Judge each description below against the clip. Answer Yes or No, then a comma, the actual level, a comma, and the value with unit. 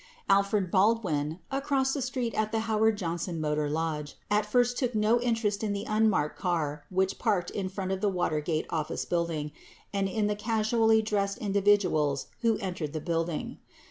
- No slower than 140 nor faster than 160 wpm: No, average, 175 wpm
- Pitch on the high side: Yes, high, 200 Hz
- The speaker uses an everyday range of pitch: Yes, average, 4.9 semitones